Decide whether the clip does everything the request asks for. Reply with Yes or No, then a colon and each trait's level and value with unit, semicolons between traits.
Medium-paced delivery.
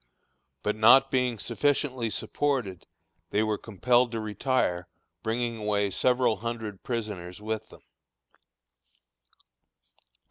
No: slow, 100 wpm